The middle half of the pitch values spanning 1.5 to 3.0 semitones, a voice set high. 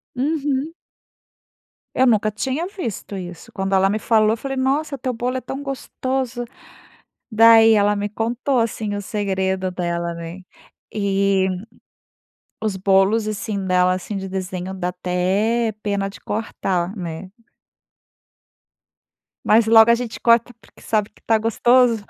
No: average, 3.8 semitones; high, 215 Hz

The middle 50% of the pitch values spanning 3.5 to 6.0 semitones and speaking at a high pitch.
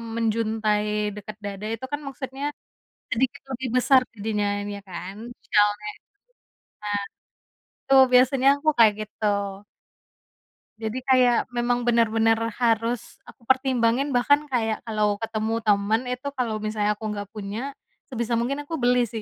No: average, 3.0 semitones; high, 230 Hz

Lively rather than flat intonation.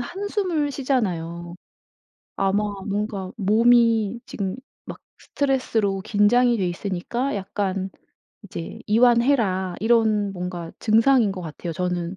No: average, 4.4 semitones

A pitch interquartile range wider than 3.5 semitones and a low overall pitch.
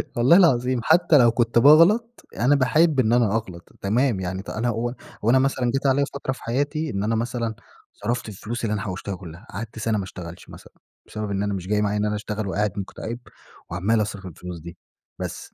Yes: average, 4.4 semitones; low, 115 Hz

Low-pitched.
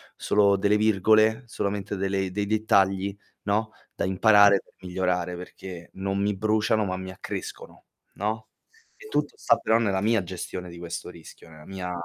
Yes: low, 100 Hz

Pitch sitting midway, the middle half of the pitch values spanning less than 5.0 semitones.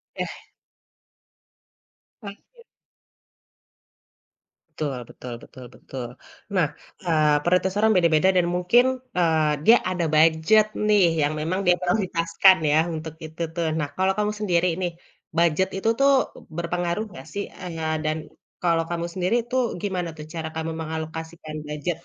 Yes: medium, 170 Hz; average, 3.0 semitones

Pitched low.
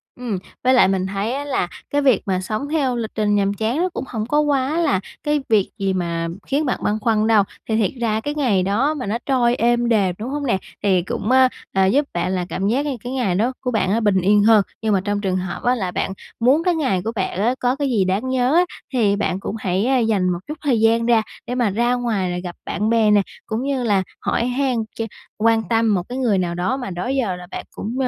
No: high, 225 Hz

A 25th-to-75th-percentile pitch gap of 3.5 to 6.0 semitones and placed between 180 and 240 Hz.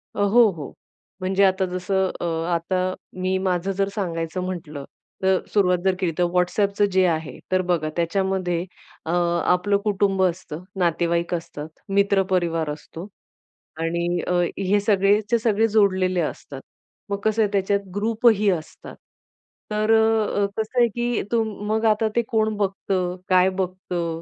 No: average, 2.7 semitones; high, 190 Hz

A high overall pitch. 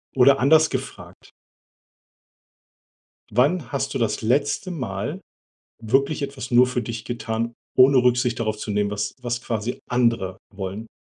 No: low, 120 Hz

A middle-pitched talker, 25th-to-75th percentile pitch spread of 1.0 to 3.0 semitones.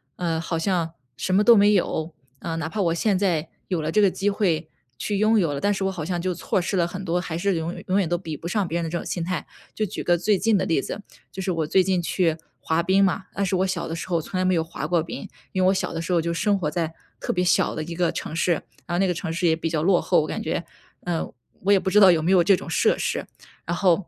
Yes: medium, 175 Hz; narrow, 2.6 semitones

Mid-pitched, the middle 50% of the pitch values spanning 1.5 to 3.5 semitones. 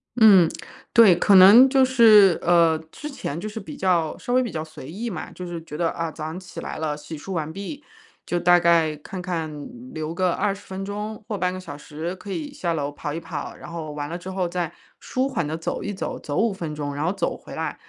No: medium, 175 Hz; average, 4.2 semitones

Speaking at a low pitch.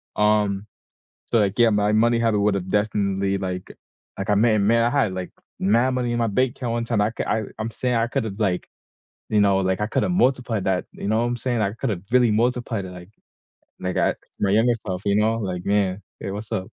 Yes: low, 105 Hz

